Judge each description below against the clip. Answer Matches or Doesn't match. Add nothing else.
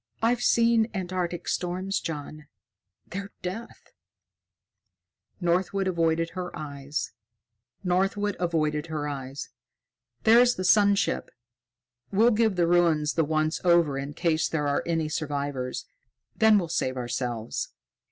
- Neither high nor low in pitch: Matches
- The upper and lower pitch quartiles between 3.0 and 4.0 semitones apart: Doesn't match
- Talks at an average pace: Doesn't match